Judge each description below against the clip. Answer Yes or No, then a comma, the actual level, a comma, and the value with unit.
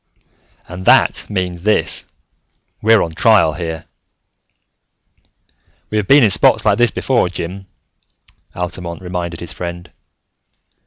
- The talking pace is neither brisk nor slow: No, slow, 115 wpm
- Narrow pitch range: No, average, 3.3 semitones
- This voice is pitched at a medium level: No, very low, 90 Hz